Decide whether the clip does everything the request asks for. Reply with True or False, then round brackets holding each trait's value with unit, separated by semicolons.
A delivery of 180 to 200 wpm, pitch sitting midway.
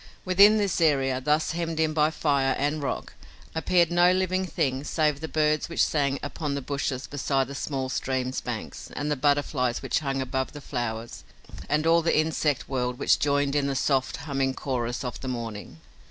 True (185 wpm; 145 Hz)